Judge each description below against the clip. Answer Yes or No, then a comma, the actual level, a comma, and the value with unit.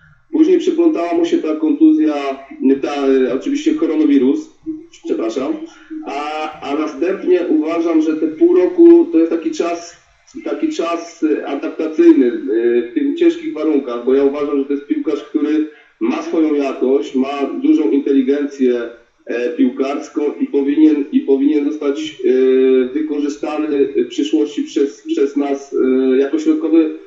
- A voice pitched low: No, medium, 160 Hz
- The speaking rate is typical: Yes, average, 125 wpm